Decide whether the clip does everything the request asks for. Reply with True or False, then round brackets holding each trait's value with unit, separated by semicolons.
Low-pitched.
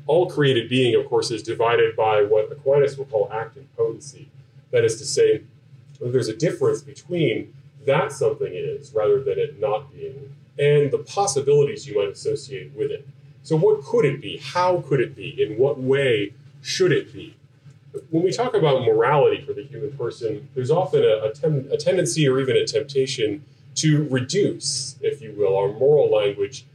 False (175 Hz)